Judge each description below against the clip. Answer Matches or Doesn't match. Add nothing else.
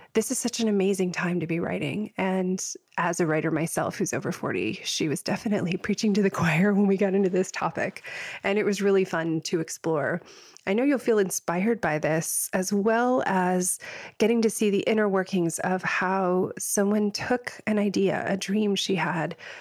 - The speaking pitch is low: Doesn't match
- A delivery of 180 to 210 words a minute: Matches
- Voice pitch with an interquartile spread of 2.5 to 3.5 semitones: Matches